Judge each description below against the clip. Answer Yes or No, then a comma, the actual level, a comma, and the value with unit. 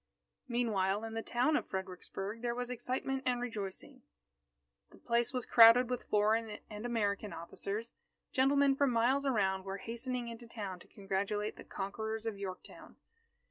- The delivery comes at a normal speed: Yes, average, 150 wpm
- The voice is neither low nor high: No, high, 225 Hz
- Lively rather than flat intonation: No, average, 3.6 semitones